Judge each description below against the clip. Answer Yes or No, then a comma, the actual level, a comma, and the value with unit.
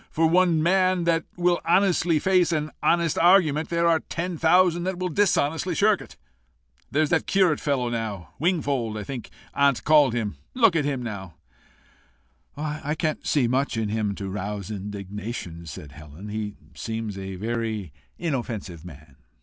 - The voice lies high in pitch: No, medium, 140 Hz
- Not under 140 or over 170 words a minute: Yes, average, 160 wpm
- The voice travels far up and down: Yes, wide, 8.5 semitones